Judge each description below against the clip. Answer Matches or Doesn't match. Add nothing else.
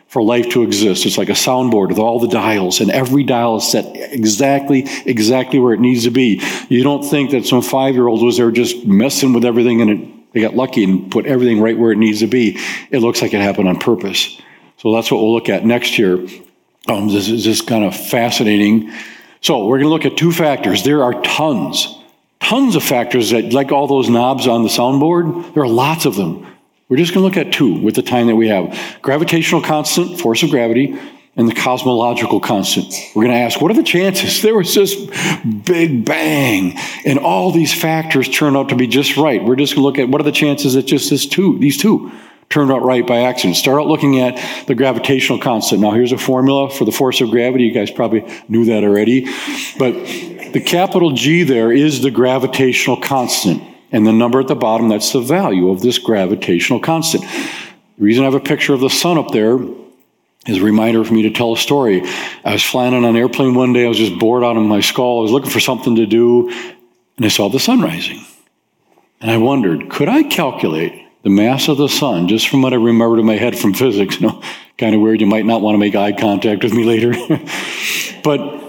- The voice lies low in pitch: Matches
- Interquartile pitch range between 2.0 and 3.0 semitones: Doesn't match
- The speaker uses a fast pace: Matches